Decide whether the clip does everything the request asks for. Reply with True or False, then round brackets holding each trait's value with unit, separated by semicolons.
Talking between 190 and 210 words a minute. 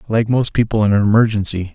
True (205 wpm)